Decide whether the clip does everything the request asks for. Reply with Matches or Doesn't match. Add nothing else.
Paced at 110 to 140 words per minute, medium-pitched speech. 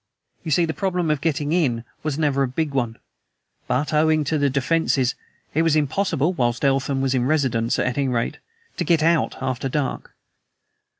Doesn't match